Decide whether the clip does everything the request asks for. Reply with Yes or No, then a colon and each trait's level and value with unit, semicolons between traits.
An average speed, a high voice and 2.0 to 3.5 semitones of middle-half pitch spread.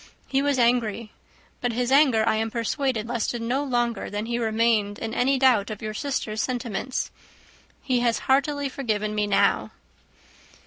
Yes: average, 160 wpm; high, 235 Hz; average, 3.1 semitones